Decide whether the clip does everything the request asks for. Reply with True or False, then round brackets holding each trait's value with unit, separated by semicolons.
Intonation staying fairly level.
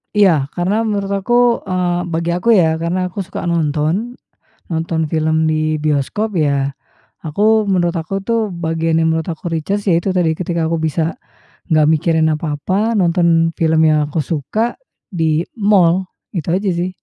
False (3.1 semitones)